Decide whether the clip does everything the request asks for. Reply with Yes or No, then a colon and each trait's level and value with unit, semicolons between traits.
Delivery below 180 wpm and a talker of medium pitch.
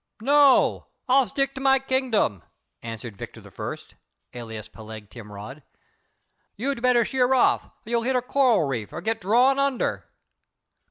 No: average, 140 wpm; high, 235 Hz